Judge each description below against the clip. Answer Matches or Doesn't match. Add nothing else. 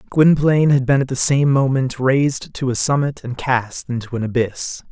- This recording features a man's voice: Matches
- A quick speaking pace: Doesn't match